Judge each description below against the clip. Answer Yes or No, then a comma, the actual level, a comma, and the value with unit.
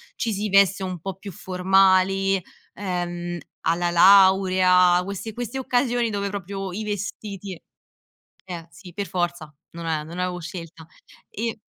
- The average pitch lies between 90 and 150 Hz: No, high, 190 Hz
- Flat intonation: Yes, narrow, 2.2 semitones